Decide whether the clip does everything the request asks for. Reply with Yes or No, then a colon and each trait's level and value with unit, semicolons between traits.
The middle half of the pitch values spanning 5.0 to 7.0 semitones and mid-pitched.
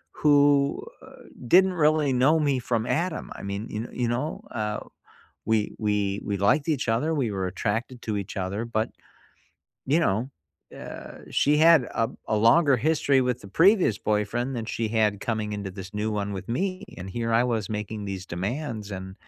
No: wide, 5.4 semitones; low, 115 Hz